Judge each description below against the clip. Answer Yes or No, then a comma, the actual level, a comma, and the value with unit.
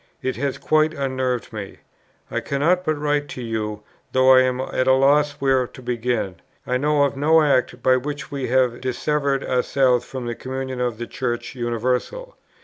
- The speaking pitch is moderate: No, low, 130 Hz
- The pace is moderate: Yes, average, 180 wpm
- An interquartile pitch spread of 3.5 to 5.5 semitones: No, narrow, 2.5 semitones